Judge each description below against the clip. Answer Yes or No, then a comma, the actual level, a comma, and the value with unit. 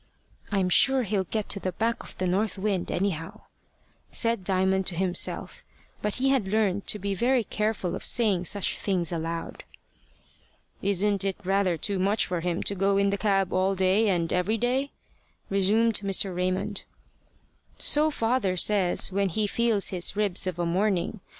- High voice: Yes, high, 195 Hz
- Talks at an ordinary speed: Yes, average, 170 wpm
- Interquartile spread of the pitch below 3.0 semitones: Yes, narrow, 2.5 semitones